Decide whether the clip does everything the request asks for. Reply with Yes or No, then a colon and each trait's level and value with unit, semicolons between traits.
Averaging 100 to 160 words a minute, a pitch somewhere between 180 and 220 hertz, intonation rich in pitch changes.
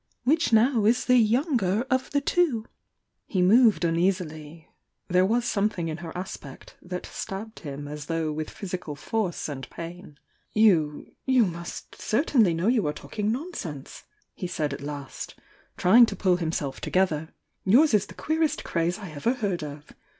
No: average, 170 wpm; medium, 185 Hz; wide, 6.2 semitones